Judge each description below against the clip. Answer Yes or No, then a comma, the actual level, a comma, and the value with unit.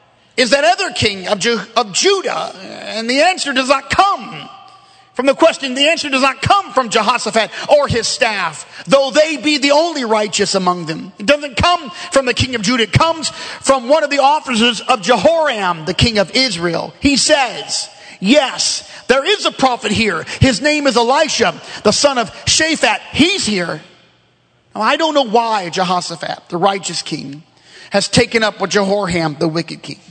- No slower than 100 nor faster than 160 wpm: No, average, 180 wpm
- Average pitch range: No, wide, 6.5 semitones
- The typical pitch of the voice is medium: No, very high, 250 Hz